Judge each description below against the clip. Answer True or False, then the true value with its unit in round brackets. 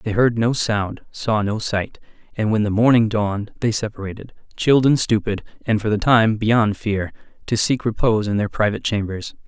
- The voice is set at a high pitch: False (110 Hz)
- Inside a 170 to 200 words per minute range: True (190 wpm)